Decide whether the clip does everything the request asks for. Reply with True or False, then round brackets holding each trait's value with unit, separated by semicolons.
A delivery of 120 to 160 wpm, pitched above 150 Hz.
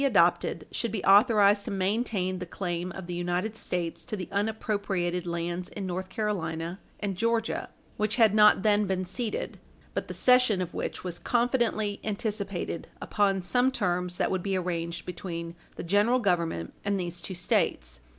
False (170 wpm; 190 Hz)